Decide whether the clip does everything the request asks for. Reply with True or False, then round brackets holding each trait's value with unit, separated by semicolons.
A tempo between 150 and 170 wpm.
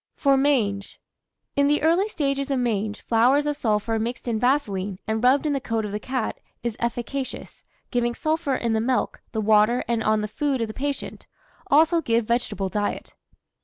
False (185 wpm)